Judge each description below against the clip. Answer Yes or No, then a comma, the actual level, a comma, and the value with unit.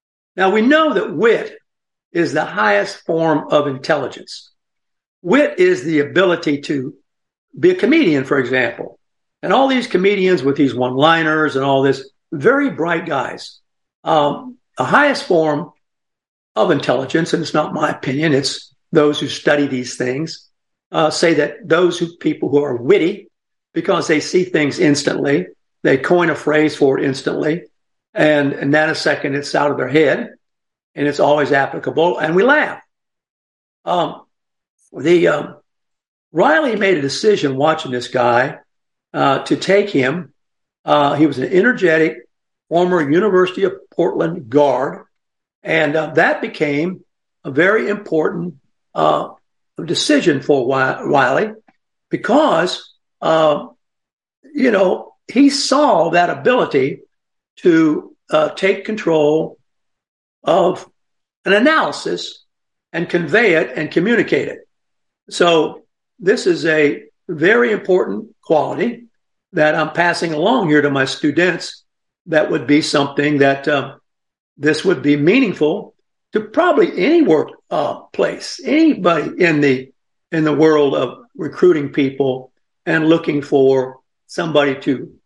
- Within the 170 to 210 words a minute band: No, slow, 135 wpm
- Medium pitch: Yes, medium, 160 Hz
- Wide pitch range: Yes, wide, 6.2 semitones